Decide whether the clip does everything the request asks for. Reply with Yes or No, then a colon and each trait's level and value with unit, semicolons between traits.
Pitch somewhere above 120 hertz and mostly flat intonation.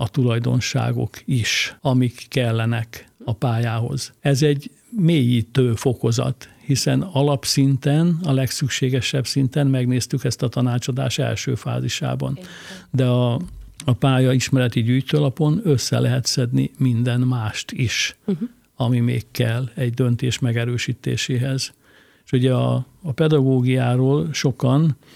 Yes: low, 130 Hz; narrow, 2.2 semitones